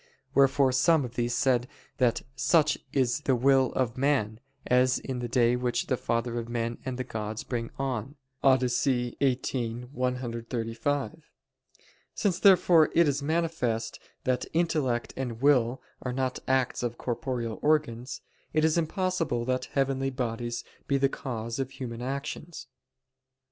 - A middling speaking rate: Yes, average, 145 wpm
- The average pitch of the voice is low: Yes, low, 130 Hz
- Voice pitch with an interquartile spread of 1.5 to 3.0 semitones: Yes, average, 2.7 semitones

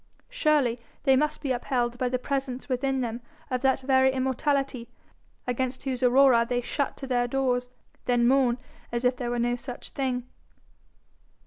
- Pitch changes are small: Yes, narrow, 1.6 semitones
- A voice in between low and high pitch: No, very high, 255 Hz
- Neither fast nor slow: Yes, average, 160 wpm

